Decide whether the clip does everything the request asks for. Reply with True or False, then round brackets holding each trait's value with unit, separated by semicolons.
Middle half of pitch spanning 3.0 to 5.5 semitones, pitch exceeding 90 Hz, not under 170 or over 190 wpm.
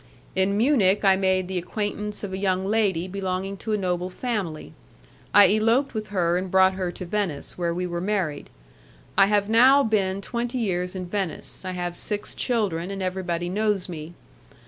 False (2.6 semitones; 190 Hz; 180 wpm)